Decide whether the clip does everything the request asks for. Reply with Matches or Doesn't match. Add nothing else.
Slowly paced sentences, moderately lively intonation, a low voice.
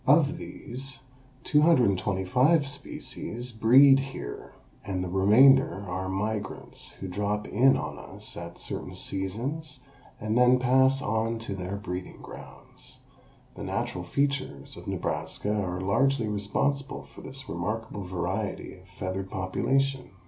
Doesn't match